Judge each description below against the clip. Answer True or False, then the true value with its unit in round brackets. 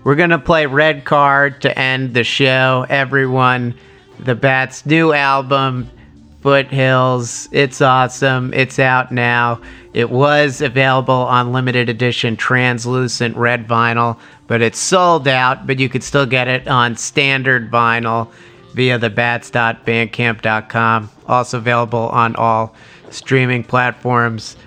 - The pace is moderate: False (125 wpm)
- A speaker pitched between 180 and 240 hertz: False (125 Hz)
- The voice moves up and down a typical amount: False (2.3 semitones)